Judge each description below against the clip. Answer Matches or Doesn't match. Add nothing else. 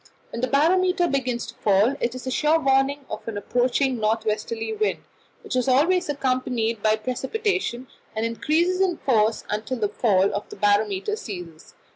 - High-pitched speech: Matches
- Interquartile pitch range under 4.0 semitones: Doesn't match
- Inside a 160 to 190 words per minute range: Matches